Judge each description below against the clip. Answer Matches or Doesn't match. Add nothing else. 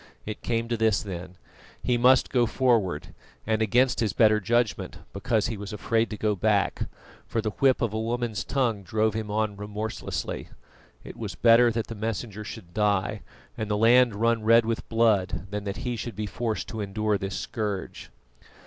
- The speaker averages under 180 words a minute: Doesn't match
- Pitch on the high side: Doesn't match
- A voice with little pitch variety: Matches